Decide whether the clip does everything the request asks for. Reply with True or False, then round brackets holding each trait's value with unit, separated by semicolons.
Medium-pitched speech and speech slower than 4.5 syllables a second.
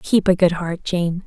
True (180 Hz; 4.3 syllables/s)